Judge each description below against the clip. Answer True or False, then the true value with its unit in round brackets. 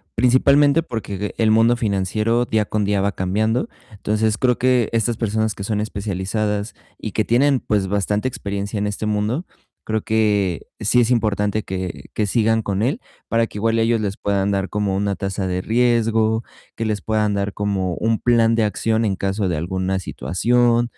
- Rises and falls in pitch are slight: True (2.3 semitones)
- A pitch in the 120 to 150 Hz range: False (110 Hz)